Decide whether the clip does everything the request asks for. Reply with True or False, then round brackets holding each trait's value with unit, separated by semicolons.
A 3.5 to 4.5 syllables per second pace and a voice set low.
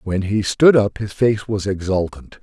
True (4.3 syllables/s; 100 Hz)